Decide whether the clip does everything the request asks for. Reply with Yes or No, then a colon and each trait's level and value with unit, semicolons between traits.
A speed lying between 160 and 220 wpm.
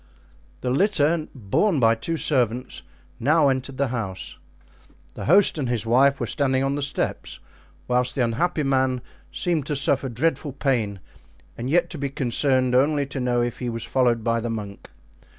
Yes: average, 170 wpm